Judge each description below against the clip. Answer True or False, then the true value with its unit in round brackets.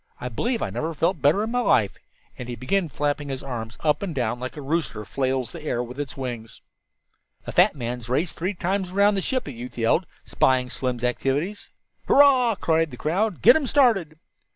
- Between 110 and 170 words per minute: False (200 wpm)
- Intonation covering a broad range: True (7.5 semitones)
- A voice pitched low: False (145 Hz)